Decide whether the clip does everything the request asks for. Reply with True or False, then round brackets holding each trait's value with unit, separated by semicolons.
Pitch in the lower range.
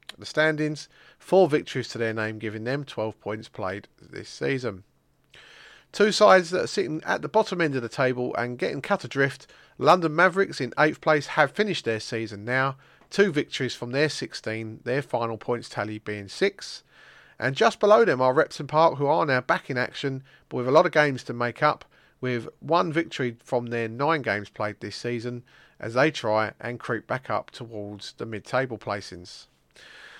True (130 Hz)